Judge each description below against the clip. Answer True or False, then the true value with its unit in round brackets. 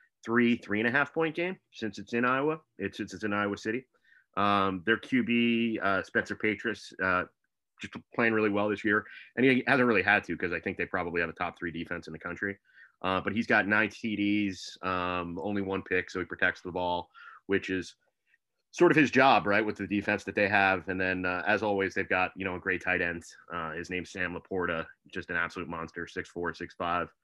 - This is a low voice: True (100 Hz)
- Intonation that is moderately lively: True (3.0 semitones)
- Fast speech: True (230 wpm)